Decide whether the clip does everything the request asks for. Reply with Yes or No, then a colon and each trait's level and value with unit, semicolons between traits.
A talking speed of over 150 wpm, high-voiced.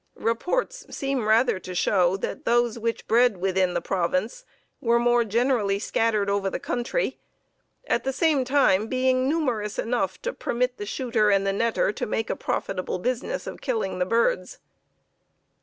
Yes: average, 160 wpm; high, 230 Hz